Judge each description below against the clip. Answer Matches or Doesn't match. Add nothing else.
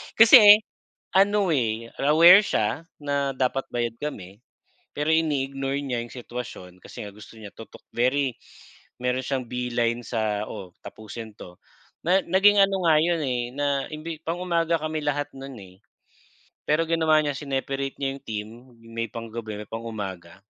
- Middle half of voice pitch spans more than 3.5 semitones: Matches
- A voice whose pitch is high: Doesn't match